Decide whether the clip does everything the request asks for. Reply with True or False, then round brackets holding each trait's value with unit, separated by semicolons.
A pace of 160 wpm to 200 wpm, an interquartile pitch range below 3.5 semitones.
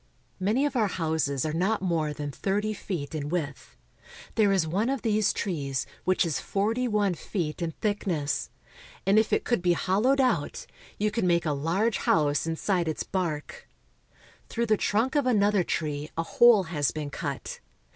False (175 wpm; 5.3 semitones)